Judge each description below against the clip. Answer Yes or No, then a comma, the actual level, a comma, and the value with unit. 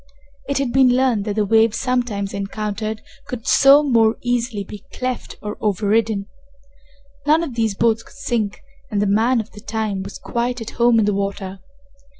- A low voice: No, high, 220 Hz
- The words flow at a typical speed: Yes, average, 175 wpm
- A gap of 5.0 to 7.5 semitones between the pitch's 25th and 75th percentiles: No, average, 3.0 semitones